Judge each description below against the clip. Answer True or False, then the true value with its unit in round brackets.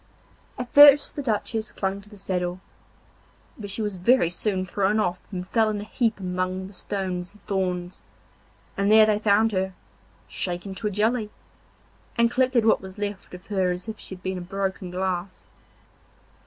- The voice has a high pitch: True (195 Hz)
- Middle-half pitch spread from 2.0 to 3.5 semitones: True (2.8 semitones)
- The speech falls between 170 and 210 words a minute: True (180 wpm)